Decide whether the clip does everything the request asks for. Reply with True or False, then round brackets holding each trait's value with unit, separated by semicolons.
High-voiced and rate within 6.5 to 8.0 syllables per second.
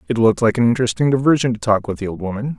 False (115 Hz; 7.9 syllables/s)